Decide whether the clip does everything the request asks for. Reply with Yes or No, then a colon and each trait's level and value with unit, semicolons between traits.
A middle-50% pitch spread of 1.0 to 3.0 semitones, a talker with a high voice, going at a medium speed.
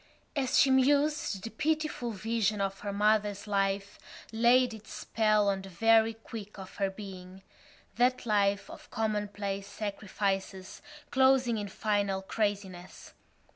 No: narrow, 2.5 semitones; high, 210 Hz; slow, 125 wpm